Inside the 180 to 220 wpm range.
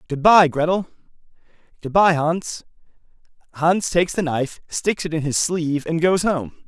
No: average, 145 wpm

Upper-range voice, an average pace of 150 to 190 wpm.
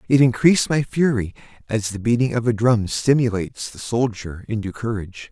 No: low, 115 Hz; average, 170 wpm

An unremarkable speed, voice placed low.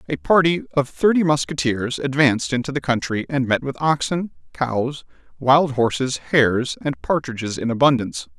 Yes: average, 150 wpm; low, 130 Hz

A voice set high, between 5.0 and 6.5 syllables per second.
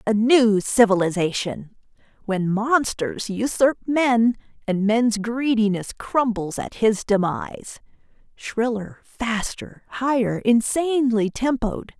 No: high, 225 Hz; 3.8 syllables/s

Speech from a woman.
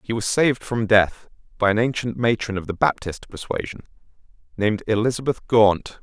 No: male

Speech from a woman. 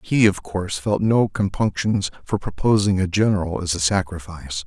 No: male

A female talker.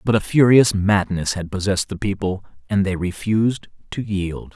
No: male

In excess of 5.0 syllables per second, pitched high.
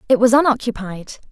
Yes: 5.8 syllables/s; high, 235 Hz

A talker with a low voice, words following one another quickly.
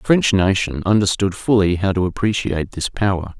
No: very low, 95 Hz; average, 175 wpm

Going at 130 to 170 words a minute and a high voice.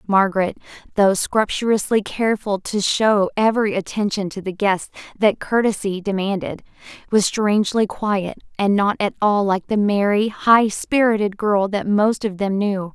Yes: average, 150 wpm; high, 205 Hz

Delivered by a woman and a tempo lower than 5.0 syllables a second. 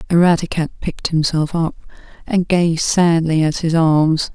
Yes: female; 4.7 syllables/s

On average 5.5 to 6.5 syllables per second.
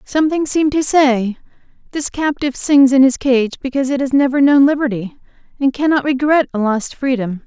Yes: 5.7 syllables/s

